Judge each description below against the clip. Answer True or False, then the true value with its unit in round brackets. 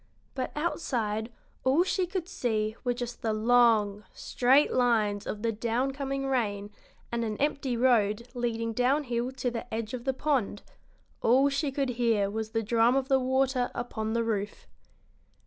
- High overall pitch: True (240 Hz)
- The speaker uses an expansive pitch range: False (3.2 semitones)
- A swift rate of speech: False (165 wpm)